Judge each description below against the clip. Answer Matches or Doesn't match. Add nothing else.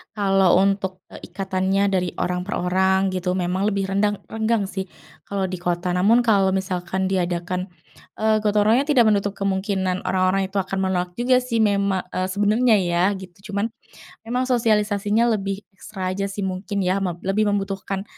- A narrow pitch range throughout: Matches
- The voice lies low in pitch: Doesn't match